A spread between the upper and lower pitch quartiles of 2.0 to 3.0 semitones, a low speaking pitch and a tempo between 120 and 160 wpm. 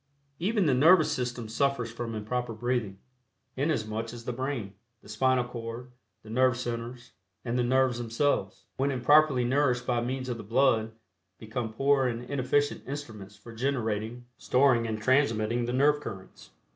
Yes: narrow, 2.6 semitones; low, 125 Hz; average, 155 wpm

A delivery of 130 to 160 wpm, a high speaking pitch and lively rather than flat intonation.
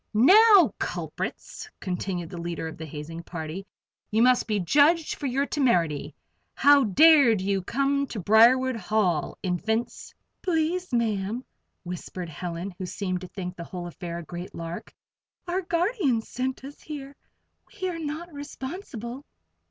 Yes: average, 145 wpm; high, 225 Hz; wide, 8.1 semitones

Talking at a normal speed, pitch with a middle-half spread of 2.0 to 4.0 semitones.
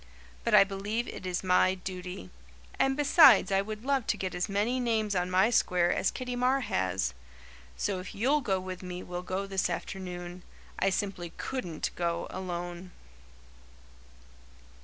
Yes: average, 160 wpm; average, 3.4 semitones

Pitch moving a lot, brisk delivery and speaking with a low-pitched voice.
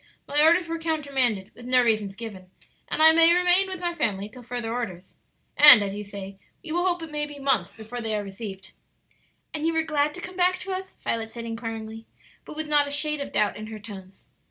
No: wide, 6.9 semitones; fast, 230 wpm; very high, 250 Hz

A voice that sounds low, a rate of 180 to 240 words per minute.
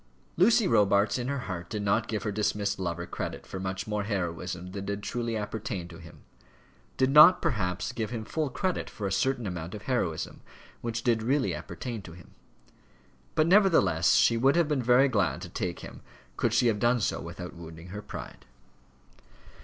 Yes: low, 105 Hz; average, 185 wpm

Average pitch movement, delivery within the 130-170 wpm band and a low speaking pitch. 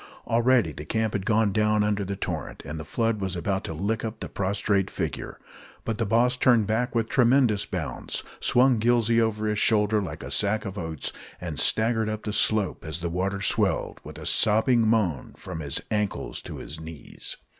No: average, 3.3 semitones; average, 195 wpm; low, 105 Hz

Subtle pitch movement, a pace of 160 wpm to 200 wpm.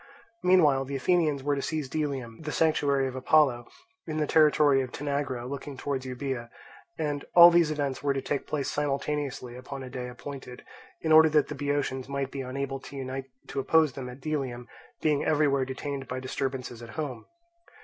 Yes: narrow, 2.2 semitones; average, 180 wpm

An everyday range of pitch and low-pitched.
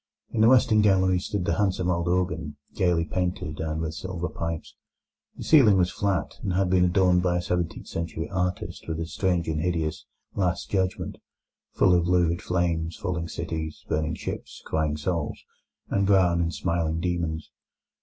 No: narrow, 2.1 semitones; very low, 90 Hz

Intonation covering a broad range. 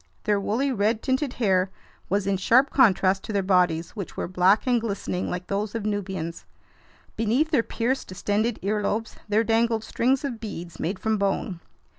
No: average, 3.3 semitones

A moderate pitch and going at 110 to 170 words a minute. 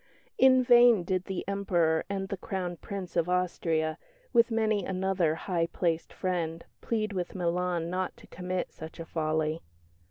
Yes: medium, 180 Hz; average, 155 wpm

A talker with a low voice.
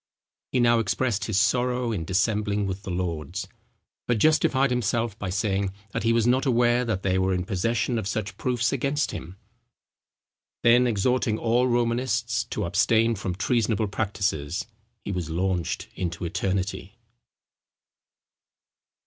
Yes: low, 110 Hz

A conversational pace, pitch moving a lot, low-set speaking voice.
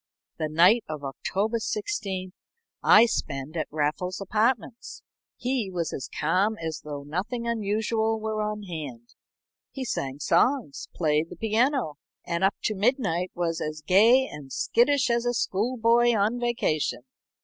No: average, 145 wpm; wide, 6.8 semitones; high, 205 Hz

